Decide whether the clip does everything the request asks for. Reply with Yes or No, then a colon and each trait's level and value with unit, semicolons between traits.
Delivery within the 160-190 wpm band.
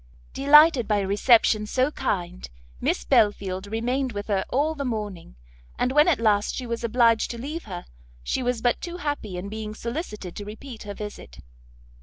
Yes: average, 180 wpm